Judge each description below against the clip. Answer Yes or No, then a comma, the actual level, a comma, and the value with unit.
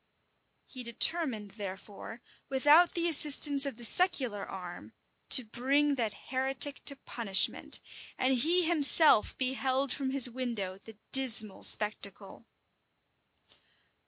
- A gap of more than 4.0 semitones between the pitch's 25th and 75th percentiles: Yes, average, 4.6 semitones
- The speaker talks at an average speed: No, slow, 110 wpm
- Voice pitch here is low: No, very high, 260 Hz